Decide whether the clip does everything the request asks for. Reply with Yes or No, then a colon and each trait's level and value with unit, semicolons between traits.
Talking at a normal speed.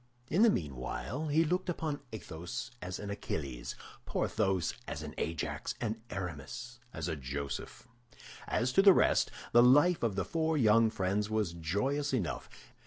Yes: average, 155 wpm